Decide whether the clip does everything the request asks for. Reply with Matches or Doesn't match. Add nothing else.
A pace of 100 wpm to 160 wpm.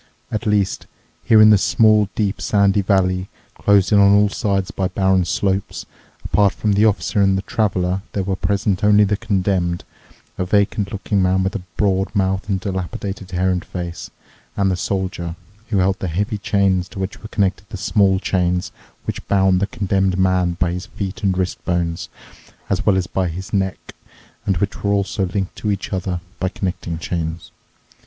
Doesn't match